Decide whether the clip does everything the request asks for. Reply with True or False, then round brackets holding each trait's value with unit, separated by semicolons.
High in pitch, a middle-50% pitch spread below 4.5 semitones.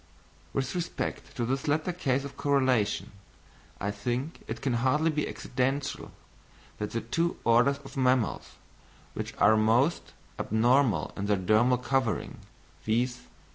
False (125 Hz; 3.6 semitones)